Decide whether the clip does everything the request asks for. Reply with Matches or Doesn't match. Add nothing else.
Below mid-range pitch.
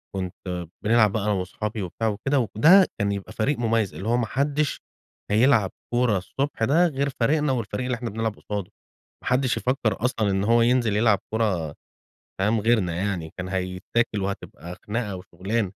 Matches